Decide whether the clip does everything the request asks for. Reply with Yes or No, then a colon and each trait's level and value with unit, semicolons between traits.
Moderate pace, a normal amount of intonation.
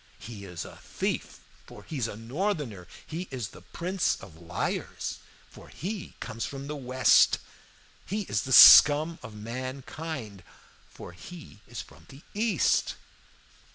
No: average, 145 wpm; wide, 6.8 semitones